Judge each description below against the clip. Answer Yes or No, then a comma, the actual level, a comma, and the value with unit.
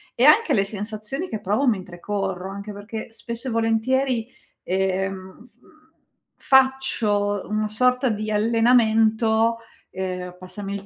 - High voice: Yes, high, 215 Hz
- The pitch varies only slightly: No, average, 3.0 semitones